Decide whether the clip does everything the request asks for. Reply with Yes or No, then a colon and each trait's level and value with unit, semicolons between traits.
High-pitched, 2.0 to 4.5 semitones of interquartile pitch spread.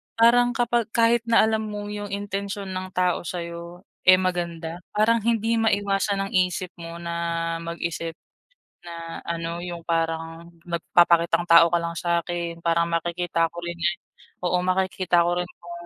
No: medium, 175 Hz; average, 2.9 semitones